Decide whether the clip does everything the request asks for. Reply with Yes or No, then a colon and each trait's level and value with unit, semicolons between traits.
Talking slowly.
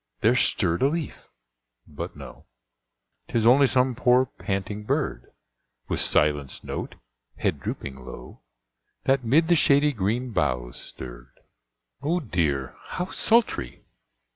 Yes: slow, 120 wpm